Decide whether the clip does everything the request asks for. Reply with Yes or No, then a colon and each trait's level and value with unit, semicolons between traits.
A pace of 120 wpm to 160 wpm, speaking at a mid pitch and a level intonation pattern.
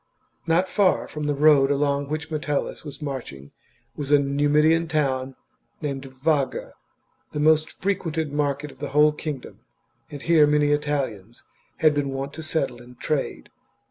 Yes: average, 155 wpm; medium, 145 Hz; narrow, 1.9 semitones